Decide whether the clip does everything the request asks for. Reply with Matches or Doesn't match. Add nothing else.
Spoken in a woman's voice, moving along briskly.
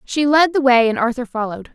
Matches